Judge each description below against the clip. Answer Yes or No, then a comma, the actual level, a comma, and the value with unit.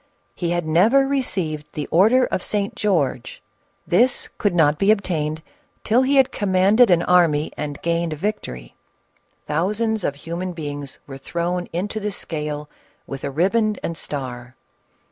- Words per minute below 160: Yes, average, 145 wpm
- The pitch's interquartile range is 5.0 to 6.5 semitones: Yes, wide, 5.6 semitones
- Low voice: No, medium, 175 Hz